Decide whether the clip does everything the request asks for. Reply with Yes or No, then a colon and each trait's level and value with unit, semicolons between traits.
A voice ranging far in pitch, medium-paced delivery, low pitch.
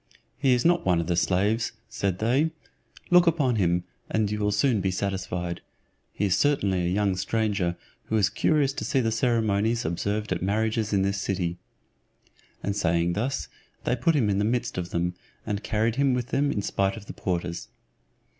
No: average, 4.2 semitones; average, 190 wpm; low, 105 Hz